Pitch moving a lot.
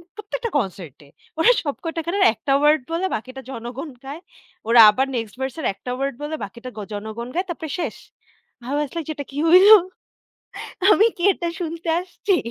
Yes: wide, 6.1 semitones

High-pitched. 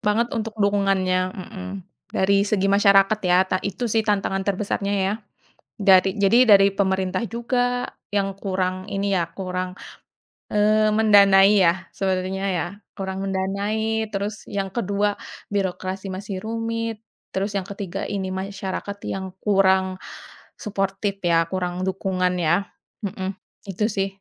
Yes: high, 195 Hz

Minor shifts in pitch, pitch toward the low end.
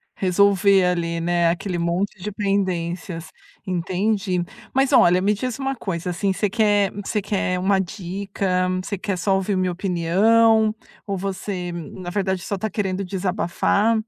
No: narrow, 2.3 semitones; high, 190 Hz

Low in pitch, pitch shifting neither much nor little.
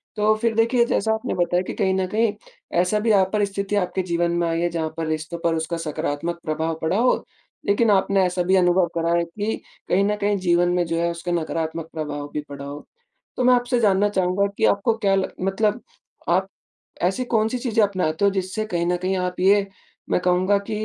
No: medium, 185 Hz; average, 3.4 semitones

